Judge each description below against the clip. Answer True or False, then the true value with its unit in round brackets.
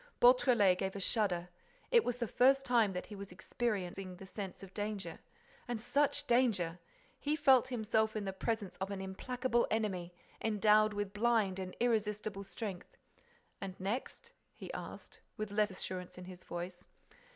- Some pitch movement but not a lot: True (3.9 semitones)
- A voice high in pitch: True (210 Hz)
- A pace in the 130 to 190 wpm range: True (160 wpm)